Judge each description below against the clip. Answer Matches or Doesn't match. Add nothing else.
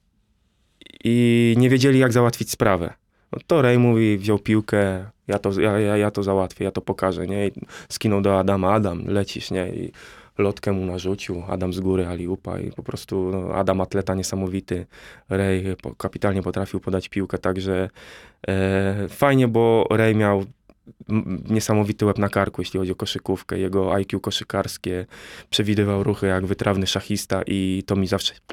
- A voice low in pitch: Matches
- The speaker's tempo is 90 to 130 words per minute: Doesn't match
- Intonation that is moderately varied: Doesn't match